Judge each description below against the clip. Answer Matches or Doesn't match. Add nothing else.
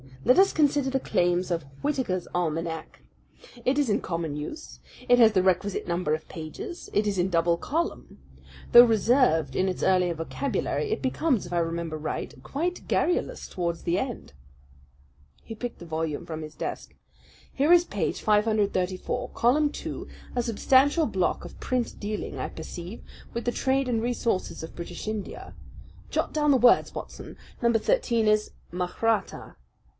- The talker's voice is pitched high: Matches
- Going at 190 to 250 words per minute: Doesn't match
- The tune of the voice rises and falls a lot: Matches